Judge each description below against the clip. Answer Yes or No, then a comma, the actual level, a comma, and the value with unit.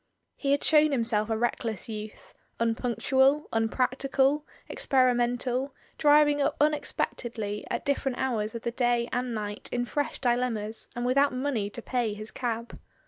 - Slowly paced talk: No, average, 155 wpm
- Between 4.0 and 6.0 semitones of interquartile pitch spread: No, average, 3.3 semitones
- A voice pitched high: Yes, high, 245 Hz